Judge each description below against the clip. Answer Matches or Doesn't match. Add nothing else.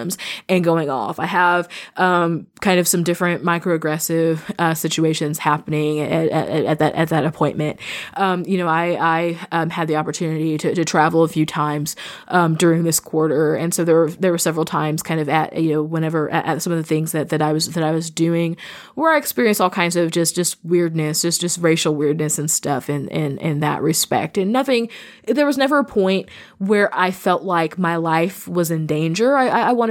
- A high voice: Doesn't match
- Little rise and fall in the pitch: Matches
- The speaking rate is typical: Doesn't match